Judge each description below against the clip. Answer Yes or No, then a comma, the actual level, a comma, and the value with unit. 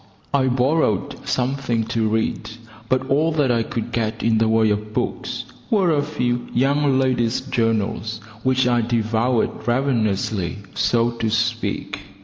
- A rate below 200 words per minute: Yes, average, 140 wpm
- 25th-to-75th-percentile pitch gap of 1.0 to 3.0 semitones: Yes, average, 2.7 semitones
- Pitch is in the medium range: No, low, 120 Hz